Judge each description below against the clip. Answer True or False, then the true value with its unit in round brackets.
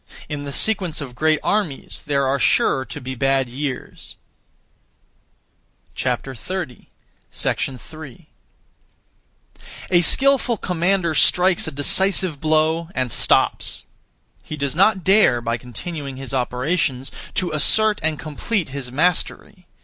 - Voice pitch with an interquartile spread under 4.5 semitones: False (5.1 semitones)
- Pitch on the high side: False (155 Hz)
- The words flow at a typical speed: False (110 wpm)